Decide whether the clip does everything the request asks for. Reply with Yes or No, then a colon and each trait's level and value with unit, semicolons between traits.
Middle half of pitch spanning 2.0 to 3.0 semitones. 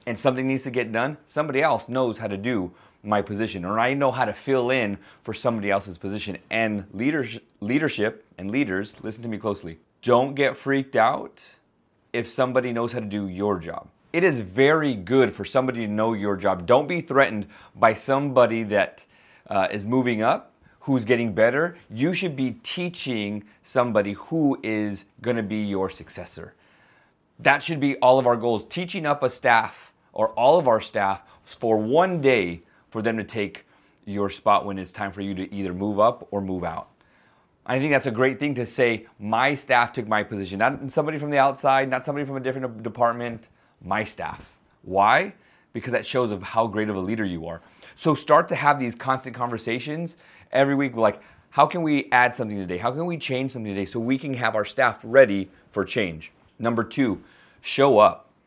No: average, 4.5 semitones